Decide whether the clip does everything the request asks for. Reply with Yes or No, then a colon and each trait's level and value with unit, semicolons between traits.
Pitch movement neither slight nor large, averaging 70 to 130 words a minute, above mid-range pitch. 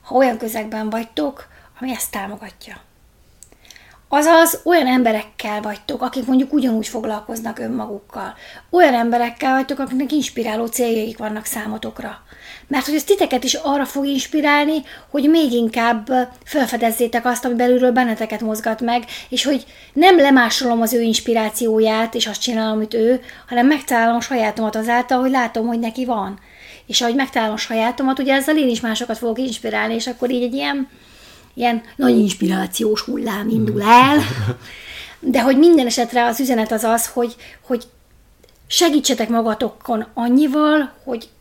No: average, 3.0 semitones; average, 145 wpm; high, 240 Hz